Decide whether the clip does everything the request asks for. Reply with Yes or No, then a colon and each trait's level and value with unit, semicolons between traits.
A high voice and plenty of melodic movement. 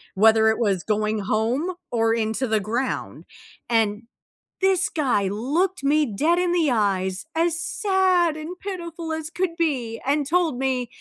Yes: very high, 270 Hz; wide, 7.5 semitones